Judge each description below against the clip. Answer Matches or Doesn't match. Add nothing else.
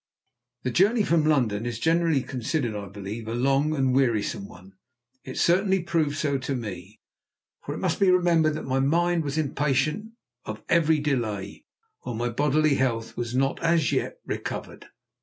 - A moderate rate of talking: Matches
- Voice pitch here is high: Doesn't match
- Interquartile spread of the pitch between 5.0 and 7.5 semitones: Matches